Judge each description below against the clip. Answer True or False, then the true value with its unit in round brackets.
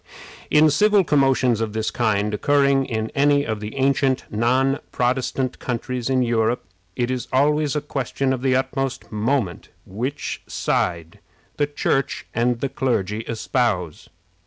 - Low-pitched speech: True (130 Hz)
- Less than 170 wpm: True (140 wpm)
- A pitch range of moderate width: True (3.4 semitones)